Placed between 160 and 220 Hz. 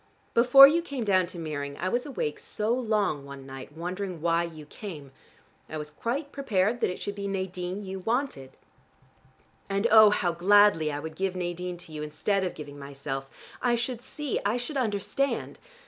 Yes: medium, 185 Hz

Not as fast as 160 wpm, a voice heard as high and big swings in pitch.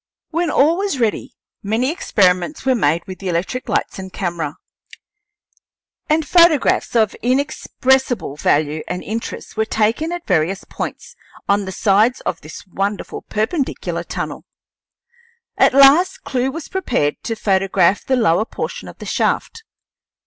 Yes: average, 140 wpm; high, 220 Hz; wide, 6.8 semitones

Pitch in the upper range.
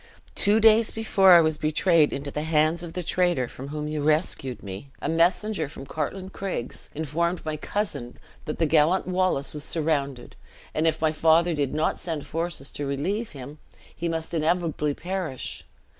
No: medium, 160 Hz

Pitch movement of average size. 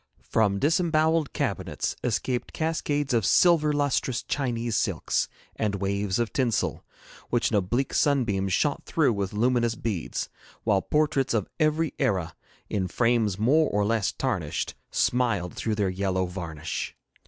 No: wide, 6.2 semitones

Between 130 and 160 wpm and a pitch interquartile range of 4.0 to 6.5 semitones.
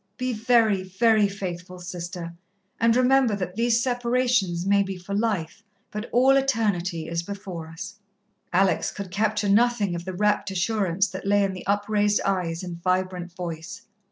No: average, 155 wpm; average, 3.5 semitones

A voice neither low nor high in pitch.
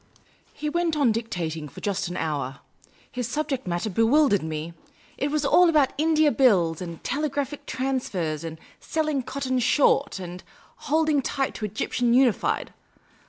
No: very high, 250 Hz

